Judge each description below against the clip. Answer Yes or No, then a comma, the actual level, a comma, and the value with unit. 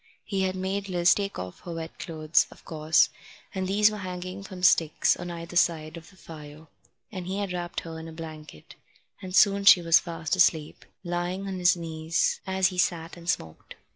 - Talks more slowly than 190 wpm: No, average, 200 wpm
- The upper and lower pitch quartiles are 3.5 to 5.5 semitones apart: No, narrow, 2.6 semitones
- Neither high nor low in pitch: Yes, medium, 175 Hz